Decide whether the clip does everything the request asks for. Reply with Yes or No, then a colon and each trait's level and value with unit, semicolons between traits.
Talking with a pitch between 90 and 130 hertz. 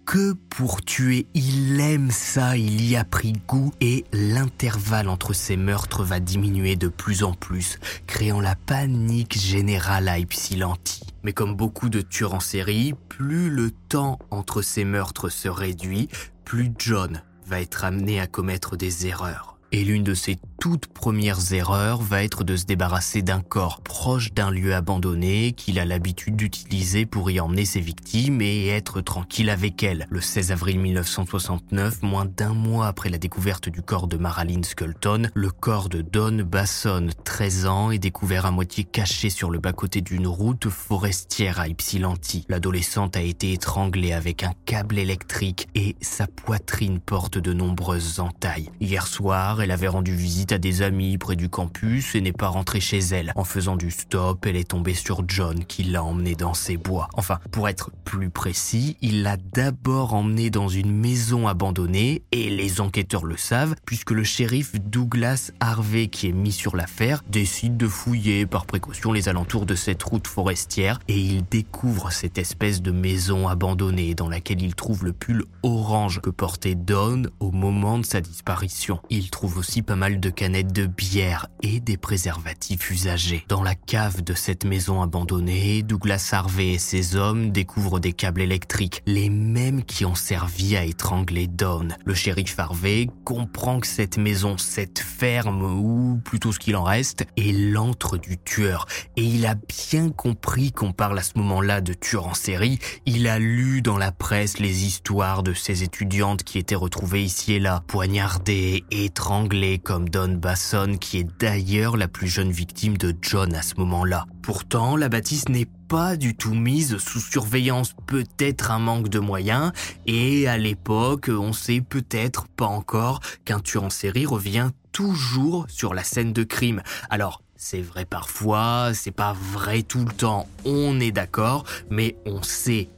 Yes: low, 100 Hz